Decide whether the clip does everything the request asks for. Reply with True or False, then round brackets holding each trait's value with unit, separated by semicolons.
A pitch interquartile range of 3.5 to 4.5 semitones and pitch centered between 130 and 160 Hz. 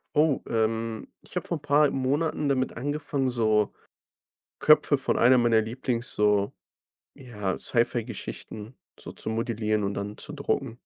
False (3.9 semitones; 120 Hz)